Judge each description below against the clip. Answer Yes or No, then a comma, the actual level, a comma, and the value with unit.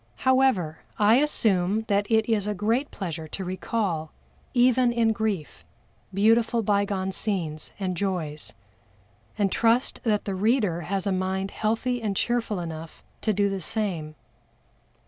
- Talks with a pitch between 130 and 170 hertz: No, high, 205 Hz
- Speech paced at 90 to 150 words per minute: Yes, average, 140 wpm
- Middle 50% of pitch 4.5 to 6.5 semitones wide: No, average, 3.5 semitones